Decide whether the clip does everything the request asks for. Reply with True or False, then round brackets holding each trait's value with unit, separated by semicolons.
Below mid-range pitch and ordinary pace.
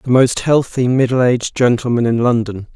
True (120 Hz; 175 wpm)